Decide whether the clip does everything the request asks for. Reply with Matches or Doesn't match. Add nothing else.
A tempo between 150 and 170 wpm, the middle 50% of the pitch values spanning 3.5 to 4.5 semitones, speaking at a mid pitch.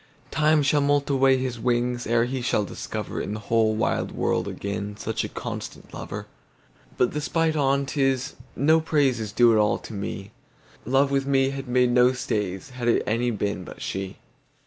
Doesn't match